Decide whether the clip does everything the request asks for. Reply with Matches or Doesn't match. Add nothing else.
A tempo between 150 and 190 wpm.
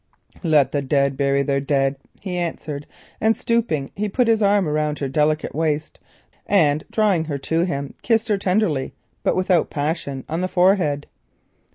Matches